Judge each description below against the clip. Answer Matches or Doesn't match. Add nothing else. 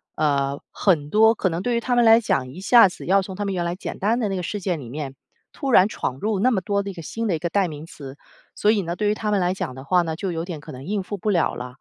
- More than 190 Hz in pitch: Doesn't match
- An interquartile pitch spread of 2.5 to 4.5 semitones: Doesn't match